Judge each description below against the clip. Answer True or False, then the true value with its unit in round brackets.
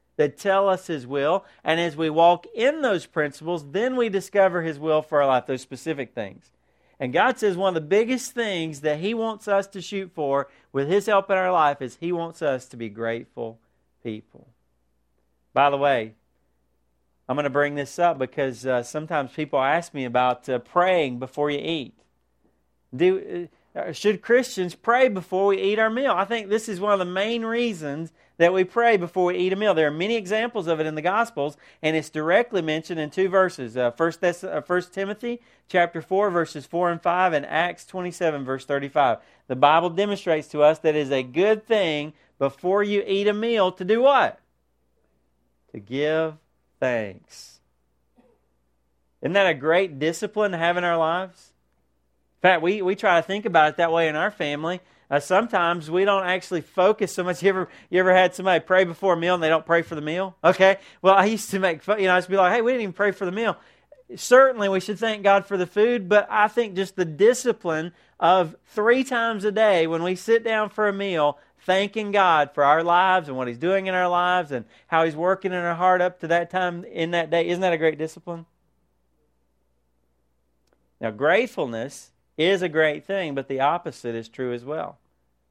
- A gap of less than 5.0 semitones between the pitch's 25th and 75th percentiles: False (5.4 semitones)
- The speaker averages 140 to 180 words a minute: False (205 wpm)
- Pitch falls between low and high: True (170 Hz)